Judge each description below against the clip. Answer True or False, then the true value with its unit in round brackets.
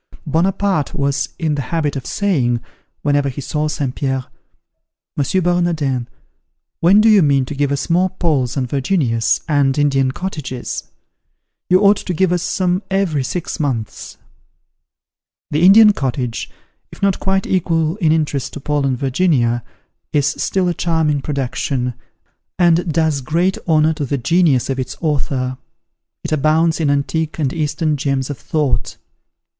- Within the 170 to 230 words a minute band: False (150 wpm)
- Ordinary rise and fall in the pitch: True (4.2 semitones)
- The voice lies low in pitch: False (150 Hz)